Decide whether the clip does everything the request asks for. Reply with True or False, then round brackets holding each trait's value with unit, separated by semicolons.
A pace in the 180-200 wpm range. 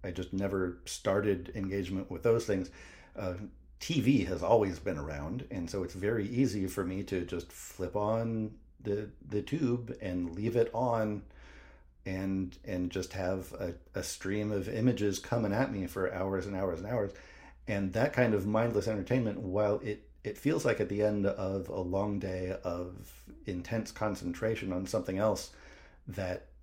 False (170 wpm)